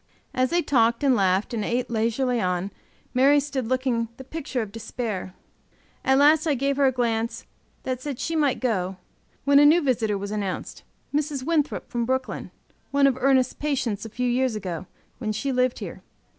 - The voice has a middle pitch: No, very high, 255 Hz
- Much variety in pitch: No, average, 3.8 semitones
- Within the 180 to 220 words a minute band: Yes, average, 185 wpm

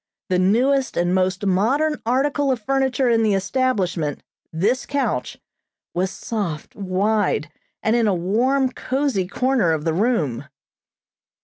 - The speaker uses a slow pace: Yes, slow, 130 wpm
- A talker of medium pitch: No, high, 215 Hz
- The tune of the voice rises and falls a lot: Yes, wide, 6.0 semitones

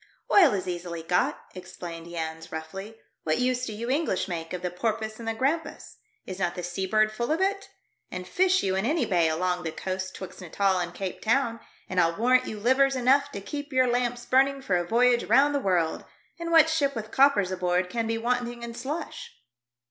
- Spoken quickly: Yes, fast, 210 wpm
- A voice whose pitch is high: Yes, high, 220 Hz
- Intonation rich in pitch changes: Yes, wide, 6.2 semitones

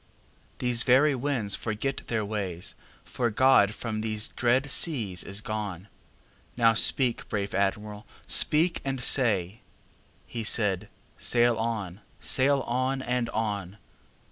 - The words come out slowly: Yes, slow, 110 wpm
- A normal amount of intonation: Yes, average, 3.6 semitones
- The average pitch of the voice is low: Yes, low, 115 Hz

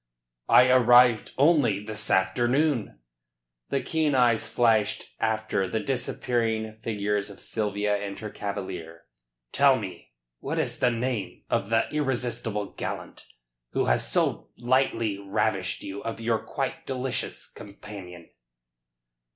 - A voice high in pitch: No, low, 110 Hz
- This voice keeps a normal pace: No, slow, 120 wpm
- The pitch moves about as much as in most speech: Yes, average, 3.4 semitones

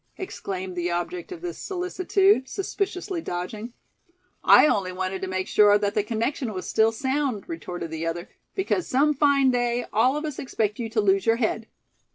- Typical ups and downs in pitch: No, wide, 7.7 semitones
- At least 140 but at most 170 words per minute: No, average, 180 wpm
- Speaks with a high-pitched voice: Yes, high, 230 Hz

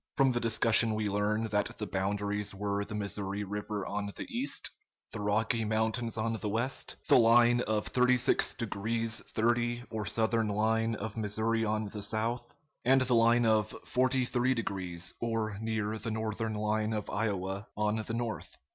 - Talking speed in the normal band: Yes, average, 165 wpm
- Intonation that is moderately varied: No, narrow, 1.9 semitones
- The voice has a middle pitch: No, low, 110 Hz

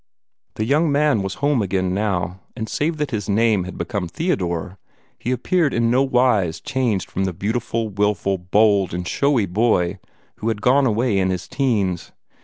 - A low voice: Yes, low, 105 Hz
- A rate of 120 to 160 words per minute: No, average, 175 wpm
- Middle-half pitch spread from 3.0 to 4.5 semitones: No, average, 5.1 semitones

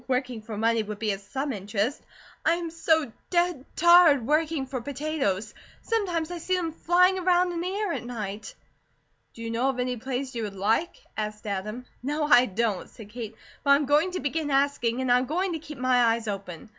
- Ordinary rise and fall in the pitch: No, wide, 6.4 semitones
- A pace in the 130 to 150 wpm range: No, fast, 205 wpm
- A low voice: No, very high, 260 Hz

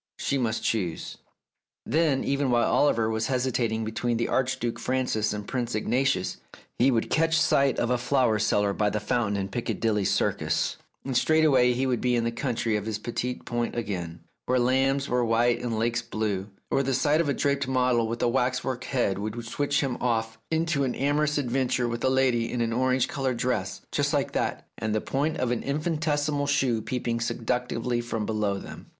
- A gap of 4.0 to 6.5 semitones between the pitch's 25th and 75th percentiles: No, average, 3.0 semitones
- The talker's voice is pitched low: Yes, low, 120 Hz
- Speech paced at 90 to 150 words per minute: No, average, 195 wpm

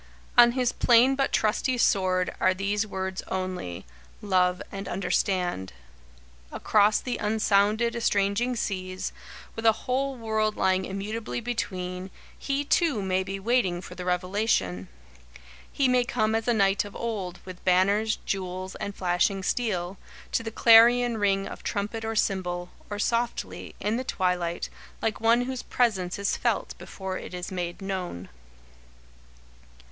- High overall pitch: Yes, high, 200 Hz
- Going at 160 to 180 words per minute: No, average, 140 wpm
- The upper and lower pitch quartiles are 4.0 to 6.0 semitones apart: No, average, 3.6 semitones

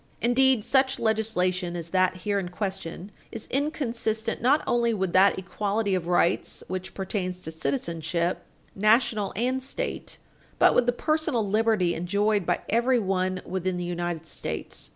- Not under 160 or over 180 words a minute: No, average, 145 wpm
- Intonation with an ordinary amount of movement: Yes, average, 4.4 semitones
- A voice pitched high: Yes, high, 200 Hz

